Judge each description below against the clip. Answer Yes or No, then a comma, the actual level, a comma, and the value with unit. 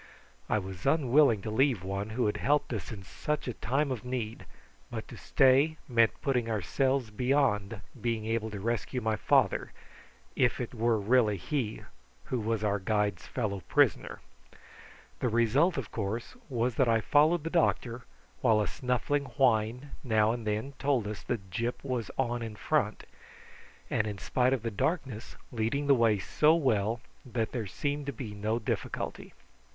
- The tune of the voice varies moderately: Yes, average, 3.6 semitones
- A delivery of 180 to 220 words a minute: No, average, 165 wpm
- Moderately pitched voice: No, low, 115 Hz